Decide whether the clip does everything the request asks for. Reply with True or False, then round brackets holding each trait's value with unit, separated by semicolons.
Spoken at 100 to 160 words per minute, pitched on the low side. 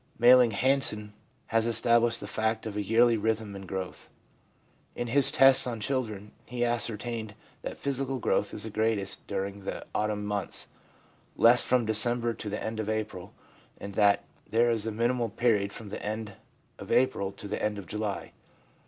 False (170 wpm; 110 Hz)